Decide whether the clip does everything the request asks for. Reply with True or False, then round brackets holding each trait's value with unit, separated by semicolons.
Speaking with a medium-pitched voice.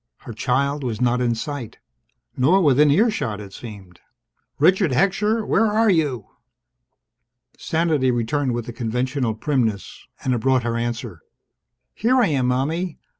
False (130 Hz)